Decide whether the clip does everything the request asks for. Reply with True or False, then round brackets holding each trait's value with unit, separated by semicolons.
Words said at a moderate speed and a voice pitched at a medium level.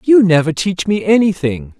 True (170 wpm; 180 Hz)